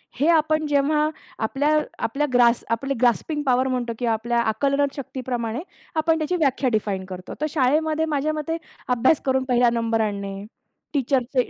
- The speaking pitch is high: Yes, very high, 260 Hz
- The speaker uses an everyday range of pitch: Yes, average, 4.3 semitones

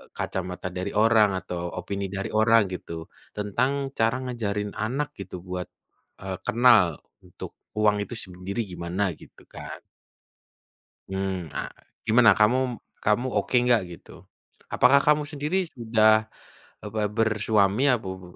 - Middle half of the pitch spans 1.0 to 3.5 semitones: No, average, 3.9 semitones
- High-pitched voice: No, low, 110 Hz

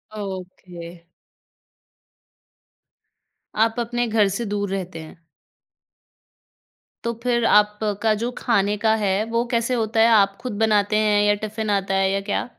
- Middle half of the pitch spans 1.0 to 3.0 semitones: Yes, narrow, 2.4 semitones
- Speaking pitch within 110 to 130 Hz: No, high, 210 Hz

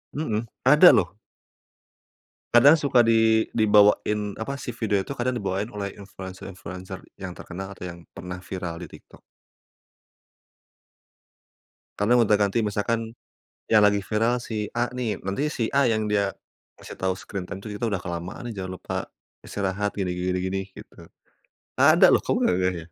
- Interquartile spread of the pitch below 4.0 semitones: Yes, average, 3.5 semitones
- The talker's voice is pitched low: Yes, low, 105 Hz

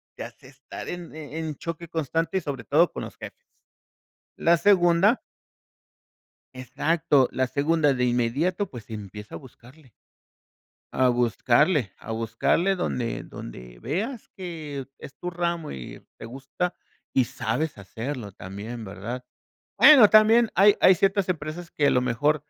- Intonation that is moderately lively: No, wide, 6.2 semitones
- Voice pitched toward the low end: No, medium, 145 Hz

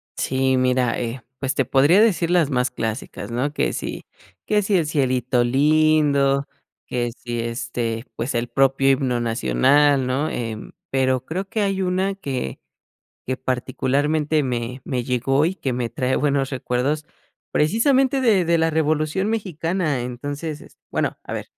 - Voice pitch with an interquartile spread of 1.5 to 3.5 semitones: No, average, 4.0 semitones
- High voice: No, low, 135 Hz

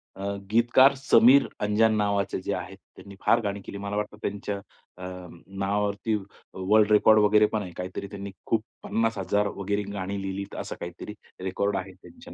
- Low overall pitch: Yes, low, 100 Hz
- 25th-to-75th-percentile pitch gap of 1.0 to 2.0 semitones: Yes, narrow, 1.7 semitones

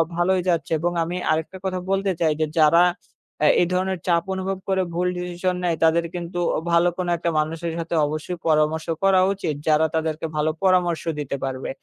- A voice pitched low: No, medium, 170 Hz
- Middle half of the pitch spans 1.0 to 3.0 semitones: Yes, narrow, 2.4 semitones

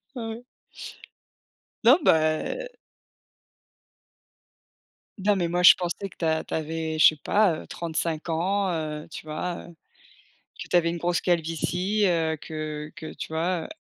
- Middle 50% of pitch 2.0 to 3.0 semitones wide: Yes, narrow, 2.6 semitones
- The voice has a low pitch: No, medium, 170 Hz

